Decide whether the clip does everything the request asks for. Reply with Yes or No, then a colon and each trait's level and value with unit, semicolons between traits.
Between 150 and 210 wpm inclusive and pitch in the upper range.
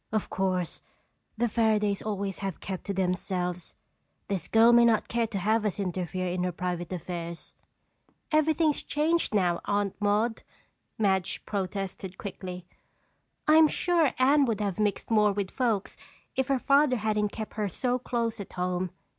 Yes: average, 155 wpm; high, 205 Hz